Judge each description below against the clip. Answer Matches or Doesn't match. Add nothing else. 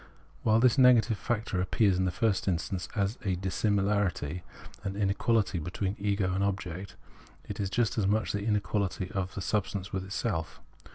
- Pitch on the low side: Matches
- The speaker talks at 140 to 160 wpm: Doesn't match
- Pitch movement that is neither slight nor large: Doesn't match